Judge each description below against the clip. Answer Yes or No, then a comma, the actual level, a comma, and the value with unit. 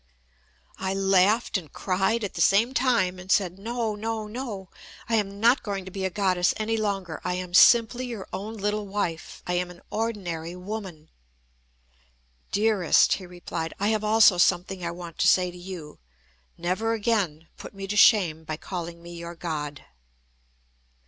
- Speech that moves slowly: No, average, 170 wpm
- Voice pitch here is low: No, high, 190 Hz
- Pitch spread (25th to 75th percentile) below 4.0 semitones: Yes, average, 3.3 semitones